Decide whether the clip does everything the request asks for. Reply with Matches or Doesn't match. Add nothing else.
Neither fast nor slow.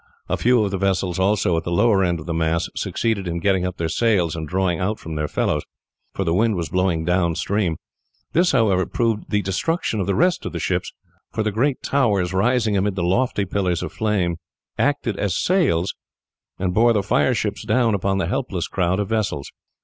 Doesn't match